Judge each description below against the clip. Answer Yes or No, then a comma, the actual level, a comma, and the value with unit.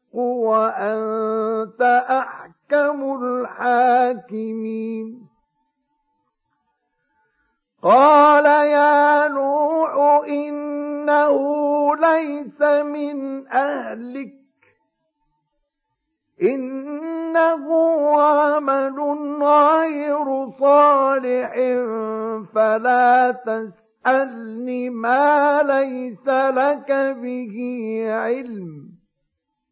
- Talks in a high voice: Yes, very high, 270 Hz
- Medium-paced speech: No, slow, 40 wpm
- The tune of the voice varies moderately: Yes, average, 3.6 semitones